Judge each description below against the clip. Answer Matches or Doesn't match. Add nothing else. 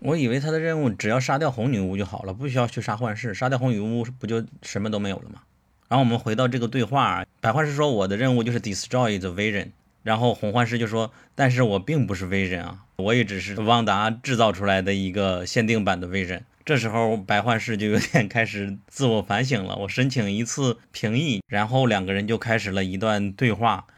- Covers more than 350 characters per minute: Matches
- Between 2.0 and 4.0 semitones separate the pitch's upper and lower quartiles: Matches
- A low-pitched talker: Matches